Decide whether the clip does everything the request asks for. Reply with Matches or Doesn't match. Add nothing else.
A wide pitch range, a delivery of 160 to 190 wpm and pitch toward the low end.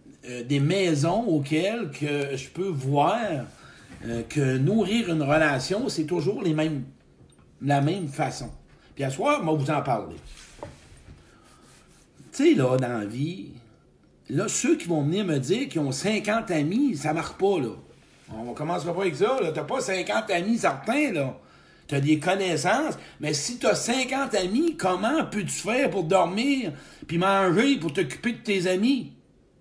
Doesn't match